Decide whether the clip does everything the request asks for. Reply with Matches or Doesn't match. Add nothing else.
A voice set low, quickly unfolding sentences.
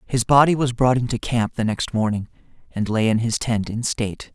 Matches